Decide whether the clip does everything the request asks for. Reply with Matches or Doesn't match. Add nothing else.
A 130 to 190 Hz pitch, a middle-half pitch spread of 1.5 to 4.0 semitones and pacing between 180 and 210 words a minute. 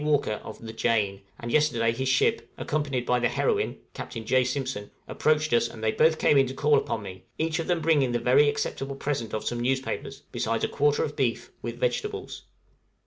Doesn't match